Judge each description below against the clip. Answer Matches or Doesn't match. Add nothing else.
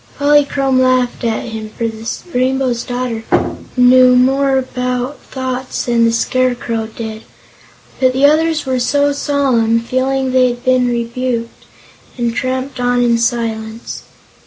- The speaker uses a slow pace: Matches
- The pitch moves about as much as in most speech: Doesn't match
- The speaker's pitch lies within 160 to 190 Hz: Doesn't match